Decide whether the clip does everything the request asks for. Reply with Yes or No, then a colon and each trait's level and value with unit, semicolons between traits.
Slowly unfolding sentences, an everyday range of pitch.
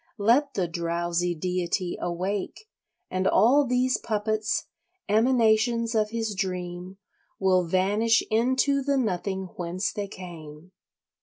Yes: slow, 110 wpm; average, 4.3 semitones